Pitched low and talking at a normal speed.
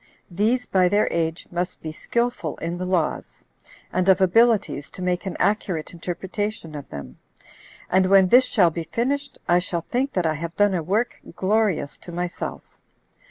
No: medium, 185 Hz; average, 170 wpm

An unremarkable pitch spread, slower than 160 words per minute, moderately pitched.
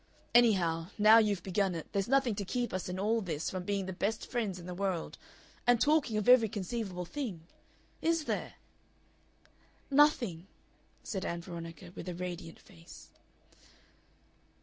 No: average, 4.5 semitones; average, 150 wpm; high, 195 Hz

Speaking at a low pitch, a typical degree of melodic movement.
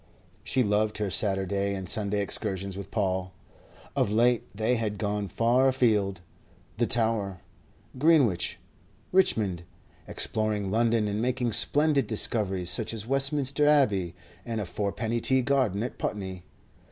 Yes: low, 110 Hz; average, 3.6 semitones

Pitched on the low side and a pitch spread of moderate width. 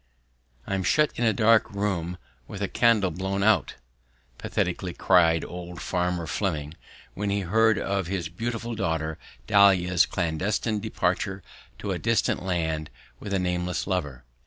Yes: very low, 95 Hz; average, 3.0 semitones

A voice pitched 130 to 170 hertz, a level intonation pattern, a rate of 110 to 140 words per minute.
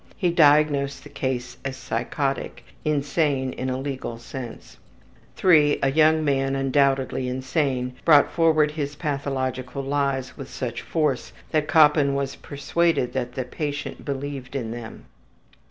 Yes: medium, 140 Hz; narrow, 2.3 semitones; slow, 135 wpm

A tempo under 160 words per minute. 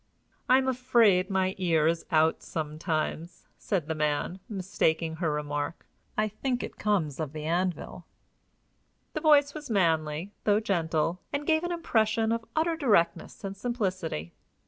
Yes: average, 145 wpm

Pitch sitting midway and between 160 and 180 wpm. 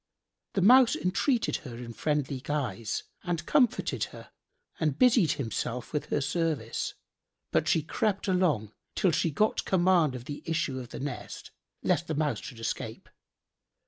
No: medium, 155 Hz; average, 150 wpm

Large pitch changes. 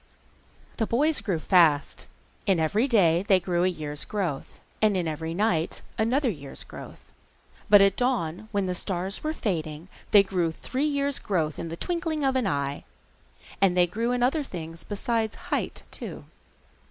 Yes: wide, 5.9 semitones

